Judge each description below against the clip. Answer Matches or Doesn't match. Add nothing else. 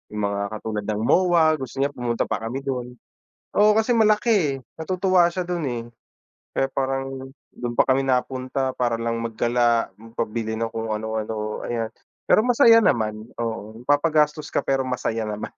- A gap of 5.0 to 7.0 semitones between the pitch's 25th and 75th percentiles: Matches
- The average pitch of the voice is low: Matches